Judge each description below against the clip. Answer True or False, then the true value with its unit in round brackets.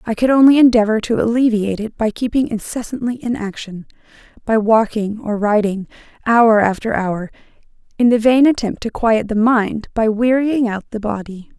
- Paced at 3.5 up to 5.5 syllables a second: True (5.2 syllables/s)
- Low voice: False (225 Hz)